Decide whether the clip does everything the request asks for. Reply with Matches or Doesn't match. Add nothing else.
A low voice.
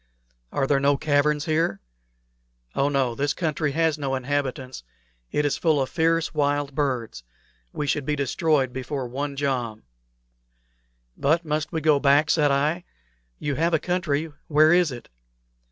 Doesn't match